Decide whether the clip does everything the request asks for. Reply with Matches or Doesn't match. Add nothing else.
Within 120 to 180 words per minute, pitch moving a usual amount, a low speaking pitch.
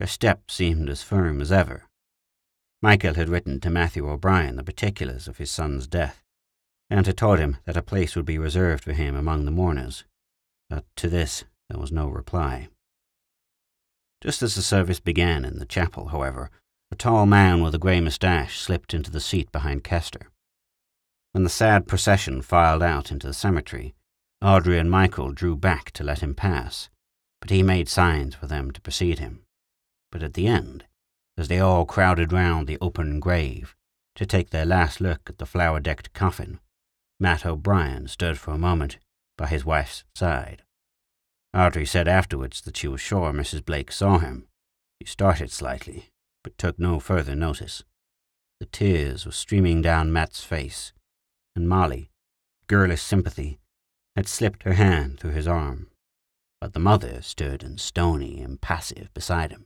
Matches